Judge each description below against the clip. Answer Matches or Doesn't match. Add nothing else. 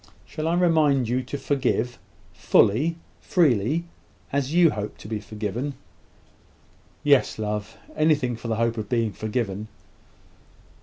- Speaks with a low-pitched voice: Matches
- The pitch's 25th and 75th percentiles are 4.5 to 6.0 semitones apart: Matches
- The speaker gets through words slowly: Matches